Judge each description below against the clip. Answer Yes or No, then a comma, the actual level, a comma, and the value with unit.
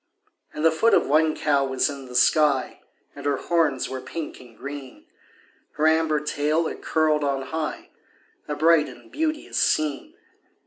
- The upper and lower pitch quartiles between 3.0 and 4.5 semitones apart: No, narrow, 2.5 semitones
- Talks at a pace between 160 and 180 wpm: Yes, average, 165 wpm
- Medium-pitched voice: Yes, medium, 150 Hz